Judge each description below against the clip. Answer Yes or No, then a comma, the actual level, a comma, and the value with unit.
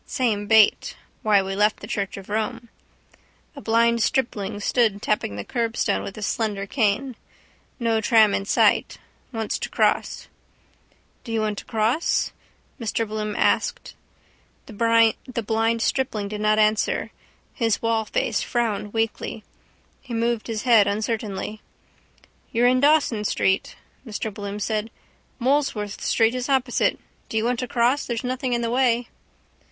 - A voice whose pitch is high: Yes, high, 225 Hz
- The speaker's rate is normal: Yes, average, 145 wpm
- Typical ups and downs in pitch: No, narrow, 2.2 semitones